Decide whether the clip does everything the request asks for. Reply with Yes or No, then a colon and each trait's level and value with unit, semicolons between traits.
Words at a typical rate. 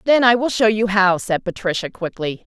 No: fast, 210 wpm